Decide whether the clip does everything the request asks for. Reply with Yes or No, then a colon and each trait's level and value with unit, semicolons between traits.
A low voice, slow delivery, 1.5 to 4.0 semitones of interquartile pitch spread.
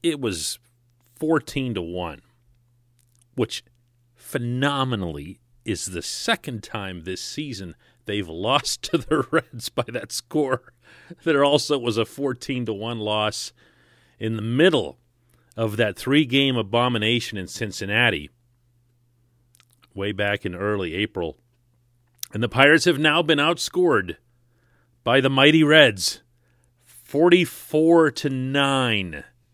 Yes: low, 120 Hz; slow, 120 wpm; average, 3.3 semitones